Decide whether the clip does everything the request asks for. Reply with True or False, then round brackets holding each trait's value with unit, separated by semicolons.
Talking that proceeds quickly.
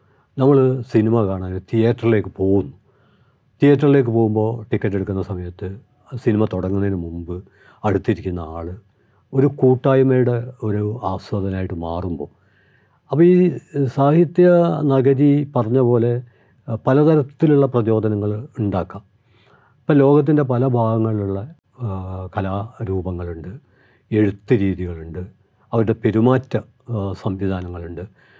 False (80 wpm)